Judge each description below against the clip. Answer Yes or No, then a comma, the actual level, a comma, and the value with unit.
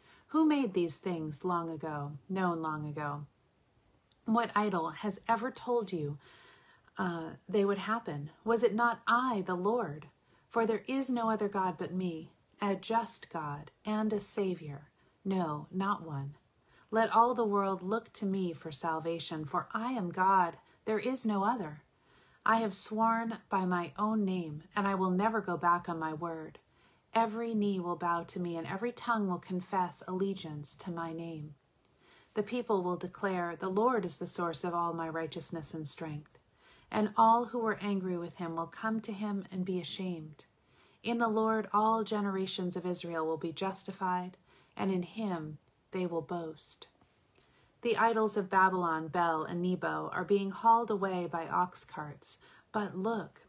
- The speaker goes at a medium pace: Yes, average, 170 wpm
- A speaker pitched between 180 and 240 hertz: Yes, medium, 185 Hz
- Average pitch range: Yes, average, 4.6 semitones